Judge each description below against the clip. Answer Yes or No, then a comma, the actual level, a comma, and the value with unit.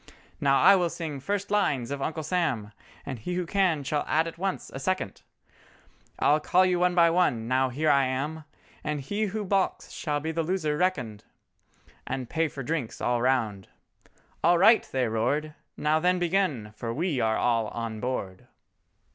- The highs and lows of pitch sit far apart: Yes, wide, 5.9 semitones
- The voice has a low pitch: No, medium, 150 Hz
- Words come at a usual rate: Yes, average, 175 wpm